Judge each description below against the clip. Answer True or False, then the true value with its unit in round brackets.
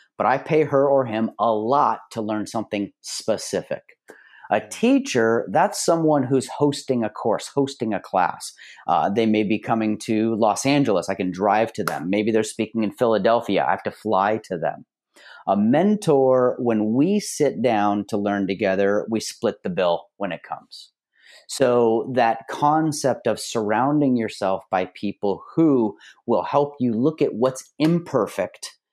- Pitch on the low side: True (115 Hz)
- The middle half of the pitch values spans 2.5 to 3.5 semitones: False (4.7 semitones)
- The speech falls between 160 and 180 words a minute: True (165 wpm)